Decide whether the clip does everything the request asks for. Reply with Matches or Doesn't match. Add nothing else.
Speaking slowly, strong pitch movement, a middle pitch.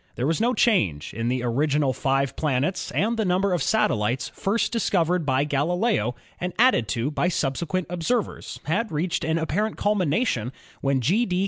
Doesn't match